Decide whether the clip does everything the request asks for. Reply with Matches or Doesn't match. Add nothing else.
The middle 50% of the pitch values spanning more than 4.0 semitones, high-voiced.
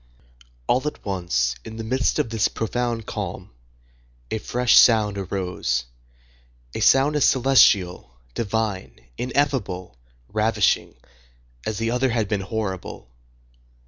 Doesn't match